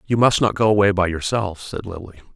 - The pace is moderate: No, fast, 230 wpm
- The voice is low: Yes, low, 100 Hz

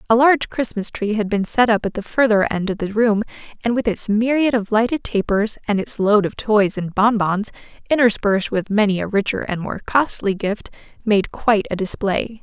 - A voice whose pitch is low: No, high, 215 Hz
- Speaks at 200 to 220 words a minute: Yes, fast, 205 wpm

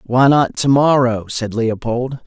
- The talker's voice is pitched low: Yes, low, 125 Hz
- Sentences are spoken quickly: No, average, 160 wpm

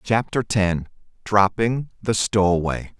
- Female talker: No, male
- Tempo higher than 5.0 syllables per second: No, 3.8 syllables/s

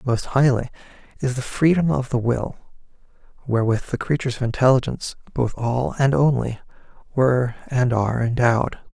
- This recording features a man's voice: Yes, male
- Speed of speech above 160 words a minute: No, average, 140 wpm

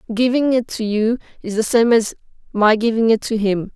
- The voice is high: Yes, high, 225 Hz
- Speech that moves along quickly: Yes, fast, 210 wpm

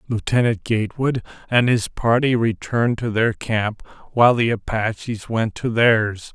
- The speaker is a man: Yes, male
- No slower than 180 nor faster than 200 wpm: No, average, 140 wpm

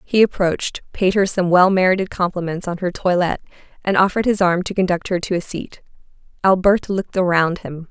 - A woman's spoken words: Yes, female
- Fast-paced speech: No, average, 190 wpm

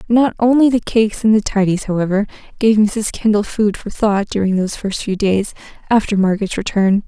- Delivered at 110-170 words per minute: No, average, 185 wpm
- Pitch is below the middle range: No, high, 210 Hz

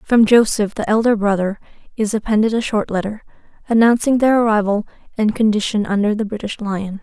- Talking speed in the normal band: Yes, average, 160 wpm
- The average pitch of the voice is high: Yes, high, 215 Hz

